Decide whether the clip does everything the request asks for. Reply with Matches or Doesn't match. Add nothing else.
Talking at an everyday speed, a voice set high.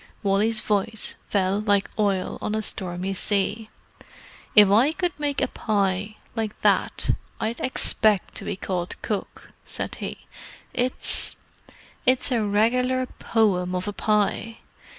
Doesn't match